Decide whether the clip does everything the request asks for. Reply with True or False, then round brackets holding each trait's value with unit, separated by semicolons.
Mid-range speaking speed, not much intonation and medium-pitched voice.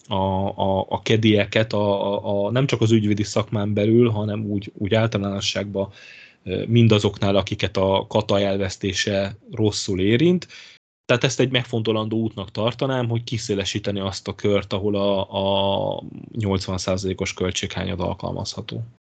False (130 wpm; 2.3 semitones; 105 Hz)